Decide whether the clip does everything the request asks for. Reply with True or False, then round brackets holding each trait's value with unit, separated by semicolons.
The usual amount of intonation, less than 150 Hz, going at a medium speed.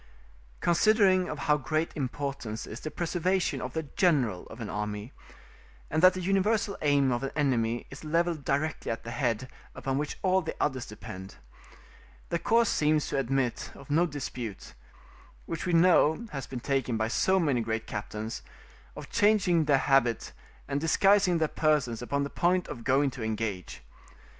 False (5.9 semitones; 140 Hz; 165 wpm)